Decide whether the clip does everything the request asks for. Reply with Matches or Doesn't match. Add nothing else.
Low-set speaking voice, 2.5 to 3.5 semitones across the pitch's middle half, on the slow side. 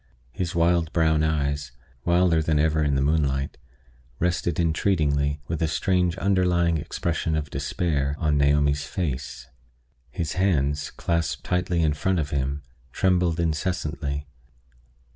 Matches